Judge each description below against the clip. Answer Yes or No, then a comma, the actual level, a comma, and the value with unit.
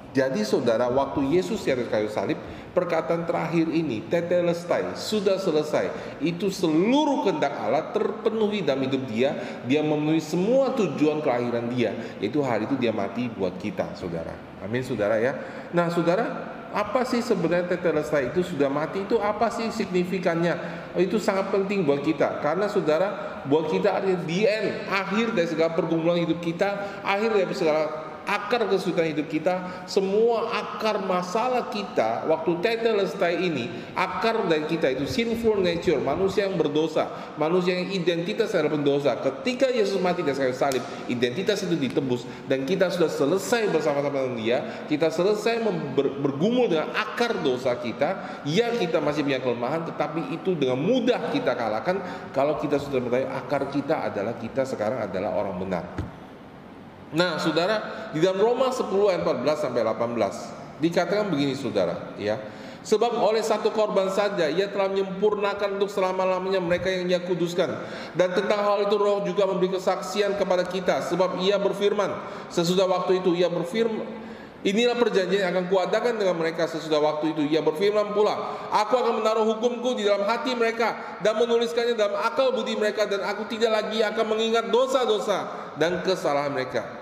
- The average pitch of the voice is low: No, medium, 185 Hz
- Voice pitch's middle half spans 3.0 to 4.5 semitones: No, average, 5.0 semitones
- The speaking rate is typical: No, fast, 155 wpm